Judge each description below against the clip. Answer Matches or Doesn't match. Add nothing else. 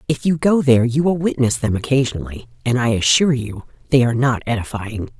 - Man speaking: Doesn't match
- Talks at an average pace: Matches